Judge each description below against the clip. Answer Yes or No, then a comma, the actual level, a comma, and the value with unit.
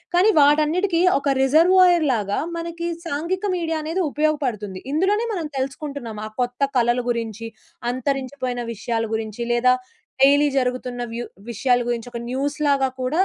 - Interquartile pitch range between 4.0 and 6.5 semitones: Yes, average, 4.7 semitones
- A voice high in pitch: Yes, very high, 275 Hz